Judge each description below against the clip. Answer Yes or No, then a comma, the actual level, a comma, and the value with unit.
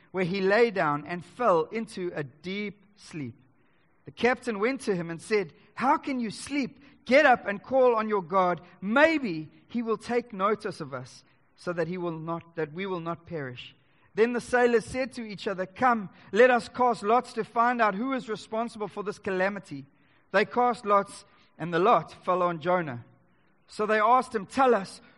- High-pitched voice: Yes, high, 200 Hz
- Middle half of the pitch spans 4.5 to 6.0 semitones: Yes, wide, 5.5 semitones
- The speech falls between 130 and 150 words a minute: No, average, 195 wpm